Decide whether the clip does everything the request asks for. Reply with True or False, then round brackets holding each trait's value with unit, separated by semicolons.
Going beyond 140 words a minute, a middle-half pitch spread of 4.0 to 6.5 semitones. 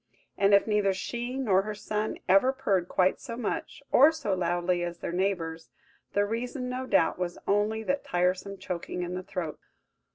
True (175 wpm; 4.4 semitones)